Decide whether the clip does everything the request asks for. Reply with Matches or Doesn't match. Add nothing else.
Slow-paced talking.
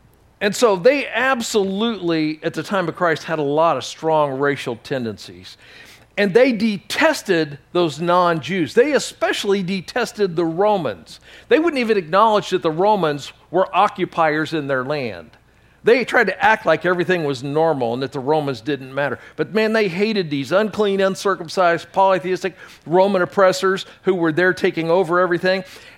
Doesn't match